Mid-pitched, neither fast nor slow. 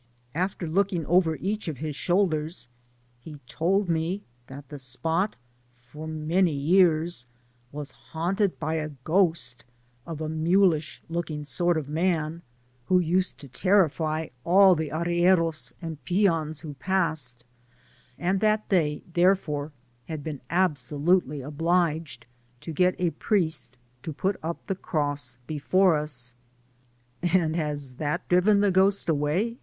No: medium, 165 Hz; slow, 130 wpm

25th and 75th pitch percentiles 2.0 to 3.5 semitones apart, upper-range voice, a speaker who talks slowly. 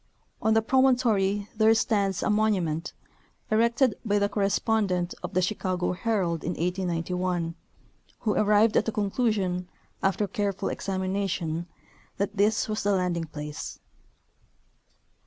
Yes: average, 3.2 semitones; high, 200 Hz; slow, 120 wpm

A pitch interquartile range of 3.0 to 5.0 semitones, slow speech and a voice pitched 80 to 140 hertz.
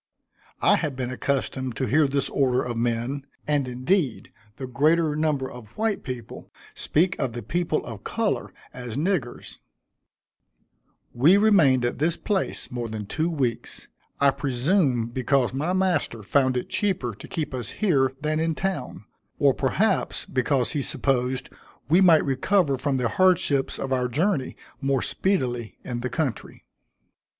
No: average, 4.3 semitones; average, 150 wpm; low, 135 Hz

